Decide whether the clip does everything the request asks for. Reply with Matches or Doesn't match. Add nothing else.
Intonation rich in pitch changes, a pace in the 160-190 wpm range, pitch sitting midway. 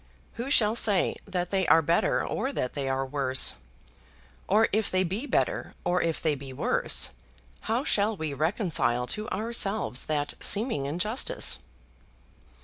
Doesn't match